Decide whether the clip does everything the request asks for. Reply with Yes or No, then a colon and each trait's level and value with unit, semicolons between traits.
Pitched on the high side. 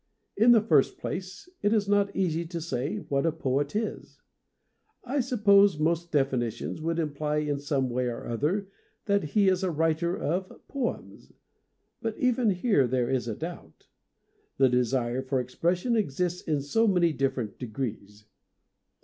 No: medium, 160 Hz